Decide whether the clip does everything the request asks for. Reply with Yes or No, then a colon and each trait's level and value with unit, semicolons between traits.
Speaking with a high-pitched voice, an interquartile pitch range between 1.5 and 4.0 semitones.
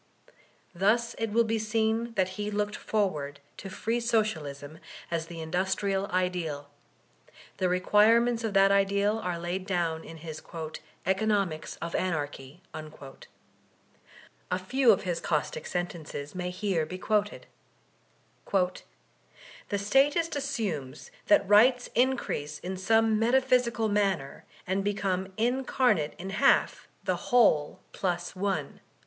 No: high, 195 Hz; average, 4.5 semitones